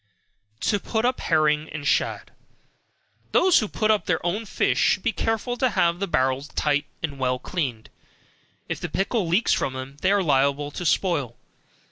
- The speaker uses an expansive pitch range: Yes, wide, 6.5 semitones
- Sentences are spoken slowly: No, average, 175 wpm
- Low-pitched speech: No, medium, 170 Hz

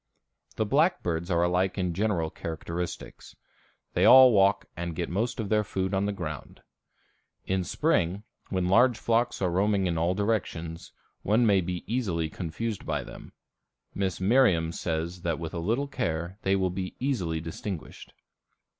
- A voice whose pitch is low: Yes, very low, 95 Hz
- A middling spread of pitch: Yes, average, 4.0 semitones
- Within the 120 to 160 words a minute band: Yes, average, 155 wpm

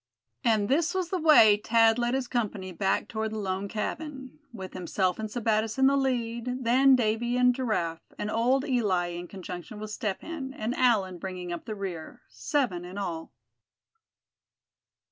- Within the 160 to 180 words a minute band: Yes, average, 165 wpm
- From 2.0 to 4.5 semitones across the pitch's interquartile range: No, average, 5.0 semitones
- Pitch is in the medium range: No, high, 220 Hz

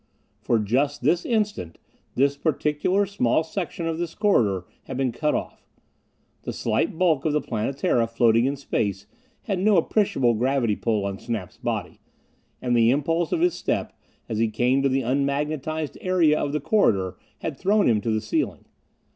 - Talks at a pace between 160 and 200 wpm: Yes, average, 170 wpm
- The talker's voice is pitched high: No, medium, 140 Hz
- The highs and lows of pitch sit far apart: Yes, wide, 6.1 semitones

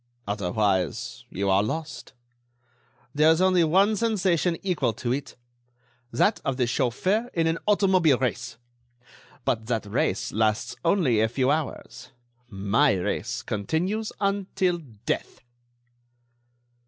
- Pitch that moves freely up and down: Yes, wide, 8.7 semitones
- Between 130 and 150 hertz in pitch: Yes, medium, 140 Hz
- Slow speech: Yes, slow, 115 wpm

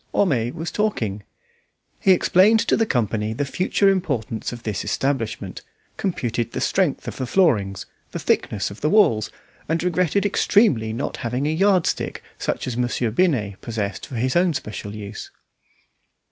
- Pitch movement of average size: No, wide, 8.5 semitones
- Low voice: Yes, low, 130 Hz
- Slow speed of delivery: No, average, 160 wpm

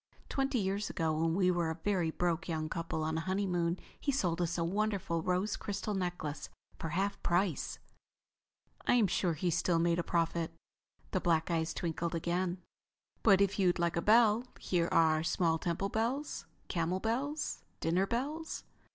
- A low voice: No, medium, 175 Hz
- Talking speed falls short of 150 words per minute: No, average, 165 wpm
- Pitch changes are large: No, average, 3.3 semitones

